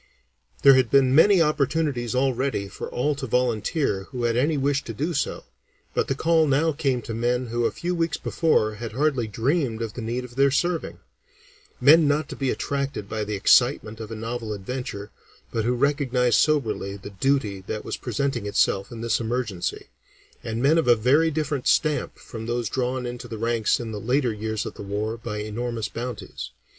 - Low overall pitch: Yes, low, 125 Hz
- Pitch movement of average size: Yes, average, 4.0 semitones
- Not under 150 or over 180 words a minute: No, average, 195 wpm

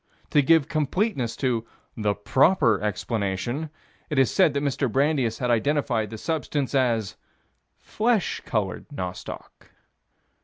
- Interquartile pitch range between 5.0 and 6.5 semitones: Yes, average, 5.3 semitones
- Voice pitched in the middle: No, low, 130 Hz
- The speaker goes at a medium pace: No, slow, 120 wpm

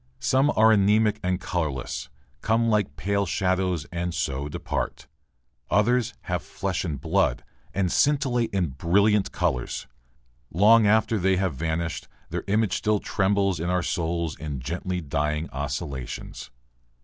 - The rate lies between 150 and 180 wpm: No, slow, 135 wpm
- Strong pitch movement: No, average, 4.4 semitones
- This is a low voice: Yes, very low, 90 Hz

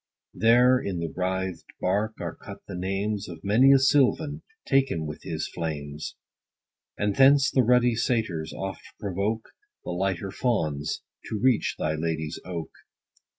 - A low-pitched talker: Yes, low, 100 Hz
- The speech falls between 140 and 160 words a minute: Yes, average, 145 wpm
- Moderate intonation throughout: No, wide, 6.7 semitones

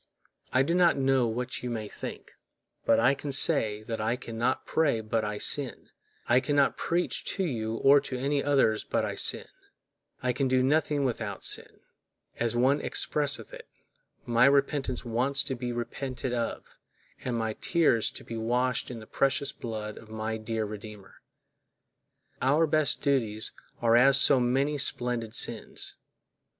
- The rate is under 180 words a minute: Yes, average, 160 wpm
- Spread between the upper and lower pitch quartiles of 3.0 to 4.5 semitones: Yes, average, 3.6 semitones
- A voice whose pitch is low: Yes, low, 125 Hz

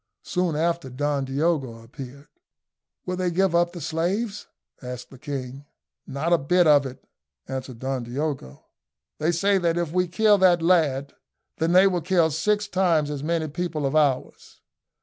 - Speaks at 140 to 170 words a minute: Yes, average, 165 wpm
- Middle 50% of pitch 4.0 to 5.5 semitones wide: Yes, average, 4.4 semitones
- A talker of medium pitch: Yes, medium, 160 Hz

